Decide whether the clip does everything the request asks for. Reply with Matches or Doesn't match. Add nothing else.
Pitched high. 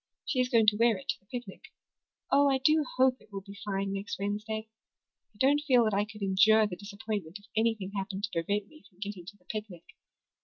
Matches